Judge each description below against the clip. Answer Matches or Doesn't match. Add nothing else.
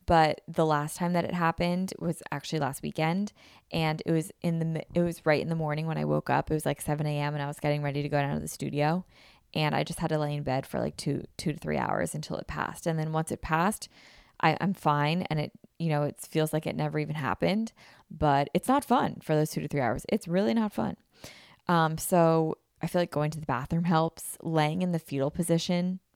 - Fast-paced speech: Matches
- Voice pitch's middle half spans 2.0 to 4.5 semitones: Matches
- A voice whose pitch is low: Doesn't match